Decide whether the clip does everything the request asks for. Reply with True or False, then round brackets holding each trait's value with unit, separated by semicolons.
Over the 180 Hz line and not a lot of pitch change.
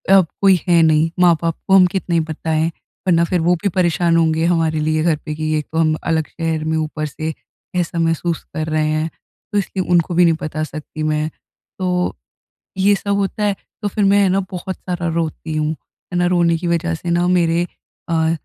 False (165 Hz; 2.2 semitones)